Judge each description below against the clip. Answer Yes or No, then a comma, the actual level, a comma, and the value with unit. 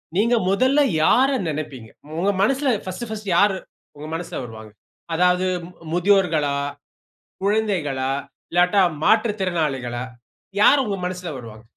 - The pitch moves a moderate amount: No, wide, 5.9 semitones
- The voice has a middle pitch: Yes, medium, 180 Hz